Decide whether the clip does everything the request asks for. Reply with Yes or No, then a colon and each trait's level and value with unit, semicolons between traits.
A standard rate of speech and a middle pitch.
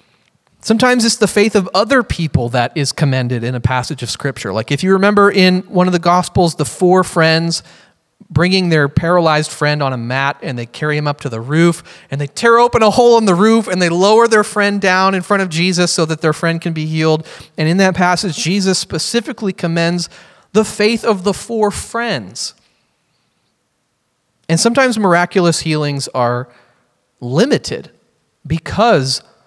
Yes: average, 180 wpm; medium, 175 Hz